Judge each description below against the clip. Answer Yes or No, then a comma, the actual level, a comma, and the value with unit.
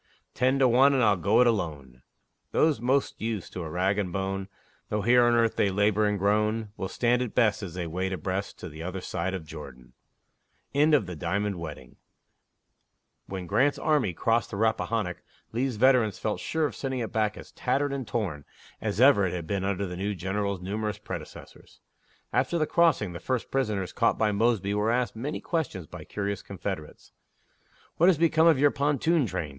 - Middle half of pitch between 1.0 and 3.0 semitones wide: No, average, 5.0 semitones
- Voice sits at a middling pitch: No, low, 105 Hz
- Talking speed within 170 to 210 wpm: Yes, average, 185 wpm